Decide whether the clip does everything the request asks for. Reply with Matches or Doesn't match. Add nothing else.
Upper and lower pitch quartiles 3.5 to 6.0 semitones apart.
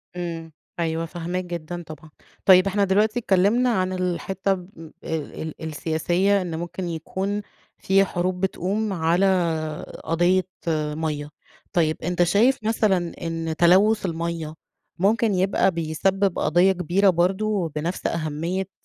Doesn't match